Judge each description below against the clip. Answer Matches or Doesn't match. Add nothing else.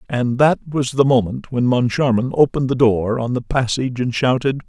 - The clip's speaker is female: Doesn't match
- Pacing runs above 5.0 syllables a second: Matches